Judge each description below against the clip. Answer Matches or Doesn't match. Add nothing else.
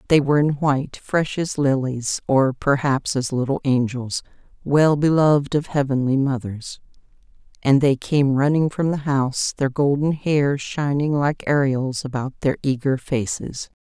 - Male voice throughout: Doesn't match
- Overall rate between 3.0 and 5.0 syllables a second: Matches